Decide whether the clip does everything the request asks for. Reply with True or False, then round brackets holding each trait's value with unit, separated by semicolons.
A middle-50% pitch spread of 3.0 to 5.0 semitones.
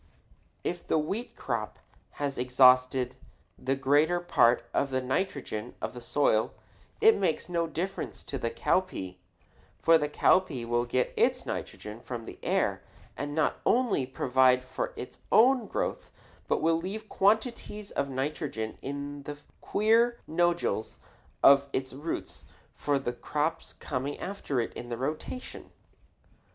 False (5.5 semitones)